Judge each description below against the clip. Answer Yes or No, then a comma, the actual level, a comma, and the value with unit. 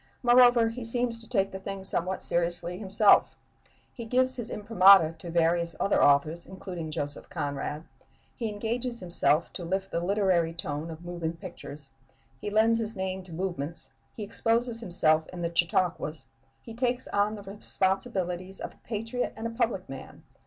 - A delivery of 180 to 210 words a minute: No, average, 165 wpm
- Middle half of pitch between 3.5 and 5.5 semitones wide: Yes, average, 4.9 semitones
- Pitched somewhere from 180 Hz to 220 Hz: Yes, high, 190 Hz